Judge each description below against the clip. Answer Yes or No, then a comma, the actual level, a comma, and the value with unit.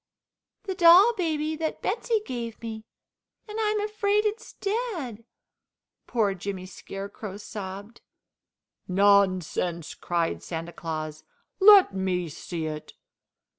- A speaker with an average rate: No, slow, 105 wpm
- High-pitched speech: Yes, high, 220 Hz